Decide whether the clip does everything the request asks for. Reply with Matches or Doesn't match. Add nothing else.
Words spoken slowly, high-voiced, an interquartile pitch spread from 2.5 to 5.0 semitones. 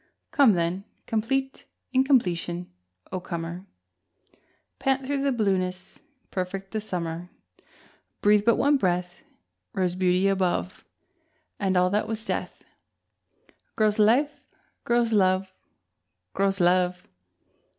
Matches